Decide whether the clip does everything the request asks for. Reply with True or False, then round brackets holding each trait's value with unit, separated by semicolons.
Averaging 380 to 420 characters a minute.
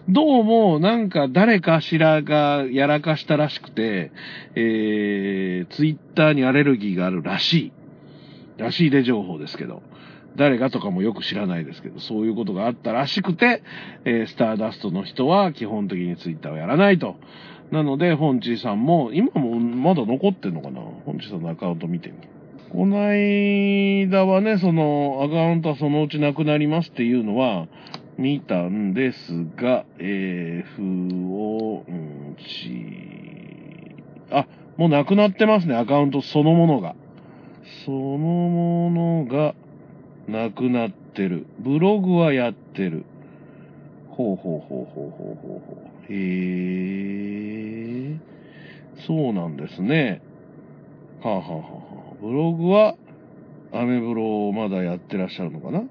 False (290 characters per minute)